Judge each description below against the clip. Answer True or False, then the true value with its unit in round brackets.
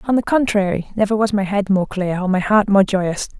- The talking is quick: True (250 wpm)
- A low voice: False (200 Hz)